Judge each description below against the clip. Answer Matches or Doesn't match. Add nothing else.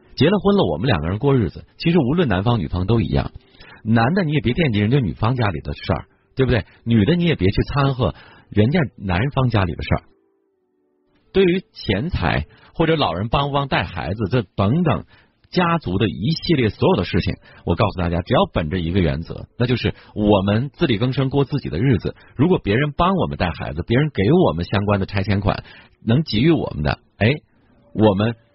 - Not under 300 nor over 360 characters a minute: Matches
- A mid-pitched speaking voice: Doesn't match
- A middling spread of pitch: Doesn't match